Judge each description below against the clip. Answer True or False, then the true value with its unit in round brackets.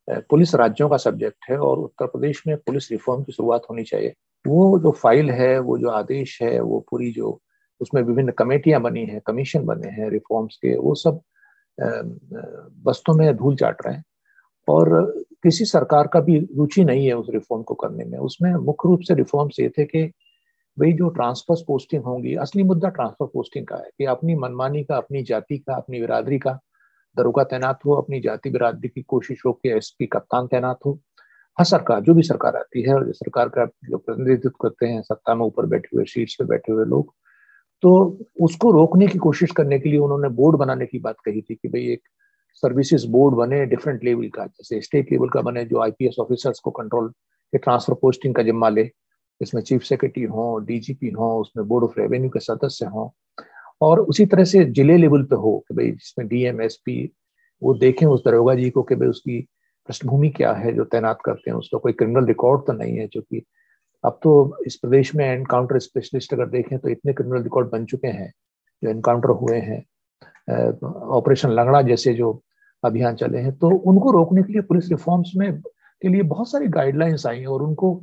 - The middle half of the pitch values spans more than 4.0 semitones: True (5.2 semitones)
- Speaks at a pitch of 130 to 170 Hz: True (135 Hz)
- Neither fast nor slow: False (200 wpm)